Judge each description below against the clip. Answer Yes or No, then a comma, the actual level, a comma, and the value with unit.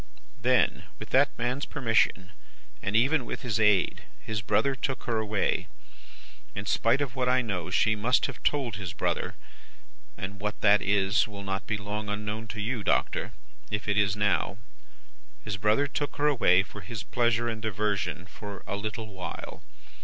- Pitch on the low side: Yes, low, 105 Hz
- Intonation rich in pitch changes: No, average, 2.8 semitones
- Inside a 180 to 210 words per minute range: No, average, 170 wpm